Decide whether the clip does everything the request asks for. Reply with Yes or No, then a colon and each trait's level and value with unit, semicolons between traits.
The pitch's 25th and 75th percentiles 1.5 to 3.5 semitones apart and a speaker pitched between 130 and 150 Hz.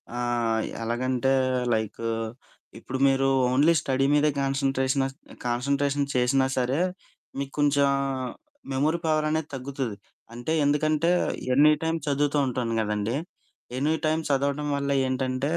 Yes: narrow, 2.4 semitones; low, 135 Hz